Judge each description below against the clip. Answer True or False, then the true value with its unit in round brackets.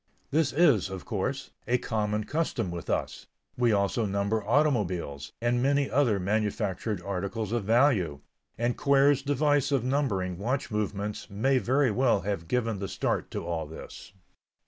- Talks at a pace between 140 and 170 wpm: True (150 wpm)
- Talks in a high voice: False (110 Hz)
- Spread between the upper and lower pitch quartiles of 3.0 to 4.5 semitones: False (5.3 semitones)